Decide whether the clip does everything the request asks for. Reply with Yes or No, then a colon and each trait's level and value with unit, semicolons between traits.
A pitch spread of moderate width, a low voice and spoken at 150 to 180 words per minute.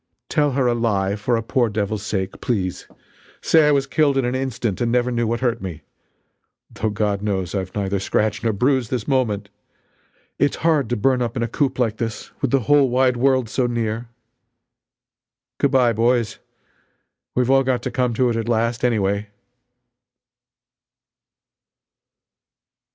Yes: average, 3.3 semitones; low, 120 Hz; average, 165 wpm